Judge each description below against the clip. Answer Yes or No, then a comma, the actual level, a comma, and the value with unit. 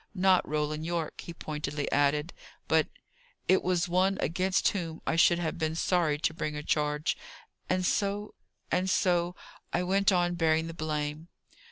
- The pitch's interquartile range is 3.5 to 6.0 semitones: No, average, 3.0 semitones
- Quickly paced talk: No, average, 160 wpm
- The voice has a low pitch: No, medium, 170 Hz